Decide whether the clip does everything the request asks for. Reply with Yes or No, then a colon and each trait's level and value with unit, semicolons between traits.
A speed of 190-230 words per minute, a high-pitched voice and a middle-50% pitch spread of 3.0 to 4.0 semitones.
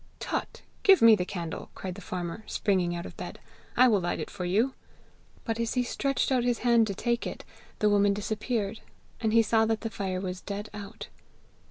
Yes: fast, 205 wpm; high, 210 Hz; average, 3.3 semitones